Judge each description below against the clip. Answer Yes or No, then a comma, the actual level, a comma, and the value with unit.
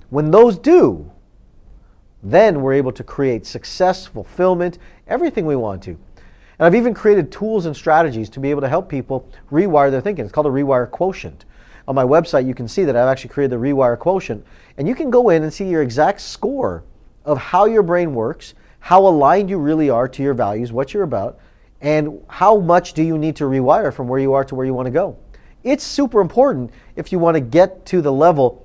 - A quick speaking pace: Yes, fast, 215 wpm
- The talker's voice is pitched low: No, medium, 150 Hz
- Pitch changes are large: Yes, wide, 5.9 semitones